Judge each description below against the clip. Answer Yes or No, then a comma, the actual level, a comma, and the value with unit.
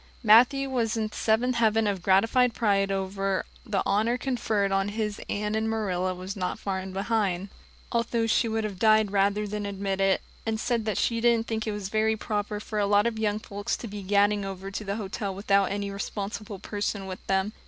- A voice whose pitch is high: Yes, high, 210 Hz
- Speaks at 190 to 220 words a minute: Yes, average, 200 wpm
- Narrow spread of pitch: Yes, narrow, 2.1 semitones